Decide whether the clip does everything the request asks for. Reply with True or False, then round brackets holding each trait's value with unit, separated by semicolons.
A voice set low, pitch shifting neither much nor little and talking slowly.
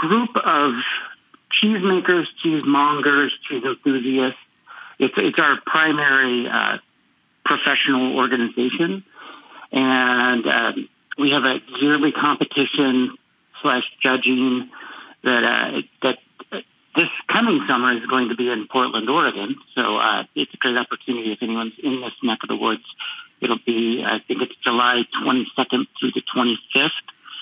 True (130 Hz; 3.2 semitones; 130 wpm)